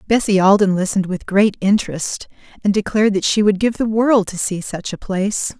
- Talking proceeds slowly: No, fast, 205 wpm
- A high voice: Yes, high, 200 Hz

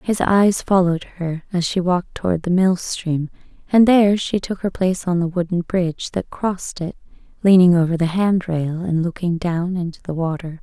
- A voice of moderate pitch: Yes, medium, 180 Hz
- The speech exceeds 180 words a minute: Yes, average, 190 wpm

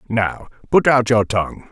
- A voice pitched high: No, low, 115 Hz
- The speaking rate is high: No, average, 175 wpm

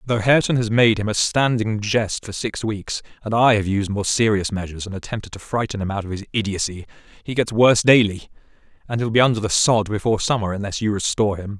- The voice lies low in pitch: Yes, low, 105 Hz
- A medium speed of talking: No, fast, 225 wpm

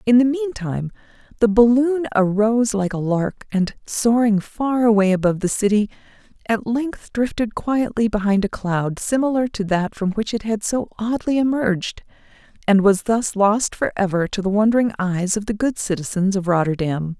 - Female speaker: Yes, female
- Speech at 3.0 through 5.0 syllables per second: Yes, 4.9 syllables/s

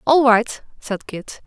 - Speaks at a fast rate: No, average, 165 wpm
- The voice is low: No, high, 235 Hz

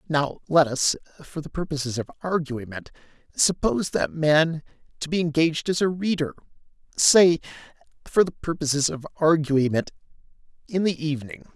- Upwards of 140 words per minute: No, slow, 135 wpm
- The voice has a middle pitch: Yes, medium, 155 Hz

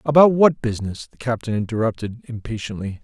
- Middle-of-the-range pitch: No, low, 115 Hz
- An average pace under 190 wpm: Yes, average, 140 wpm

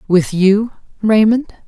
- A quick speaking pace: No, slow, 105 wpm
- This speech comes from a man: No, female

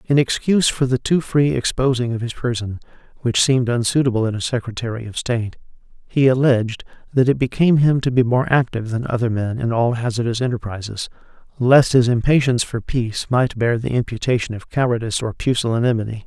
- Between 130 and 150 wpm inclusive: No, average, 175 wpm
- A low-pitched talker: Yes, low, 120 Hz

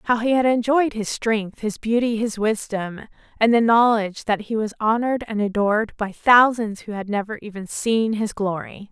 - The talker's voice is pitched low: No, high, 220 Hz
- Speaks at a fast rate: No, average, 190 wpm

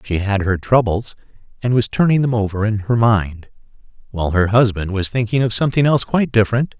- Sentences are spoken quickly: No, average, 195 wpm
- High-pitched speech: No, low, 110 Hz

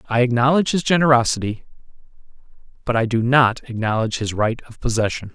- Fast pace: No, average, 145 wpm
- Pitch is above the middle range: No, low, 120 Hz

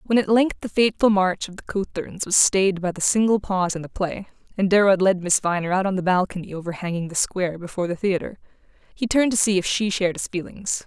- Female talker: Yes, female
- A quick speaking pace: Yes, fast, 240 wpm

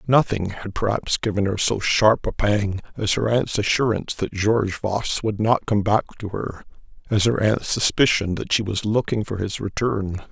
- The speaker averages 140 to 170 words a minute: No, average, 190 wpm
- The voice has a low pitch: Yes, low, 105 Hz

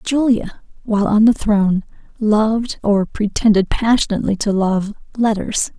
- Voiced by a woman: Yes, female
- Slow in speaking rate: Yes, slow, 125 wpm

